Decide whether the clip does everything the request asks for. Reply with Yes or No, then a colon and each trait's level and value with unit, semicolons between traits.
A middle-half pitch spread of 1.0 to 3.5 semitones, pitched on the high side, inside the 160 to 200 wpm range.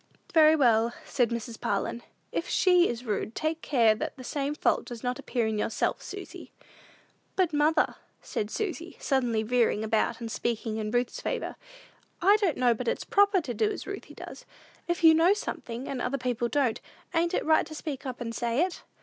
No: wide, 5.6 semitones; very high, 250 Hz; average, 190 wpm